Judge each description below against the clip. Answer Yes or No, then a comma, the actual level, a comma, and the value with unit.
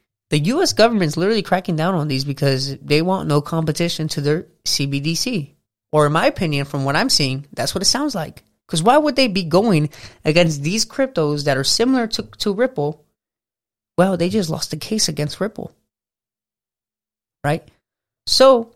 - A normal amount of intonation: No, wide, 5.9 semitones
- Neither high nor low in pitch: Yes, medium, 165 Hz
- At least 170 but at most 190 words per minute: Yes, average, 175 wpm